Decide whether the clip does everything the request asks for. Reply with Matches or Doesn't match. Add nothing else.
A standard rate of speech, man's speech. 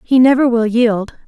Doesn't match